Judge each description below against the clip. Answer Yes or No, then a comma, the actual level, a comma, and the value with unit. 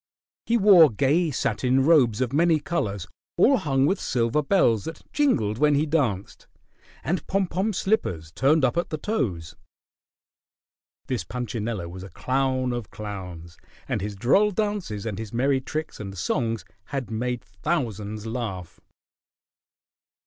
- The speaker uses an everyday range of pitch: No, wide, 7.2 semitones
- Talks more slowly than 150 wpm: Yes, average, 140 wpm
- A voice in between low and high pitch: No, low, 125 Hz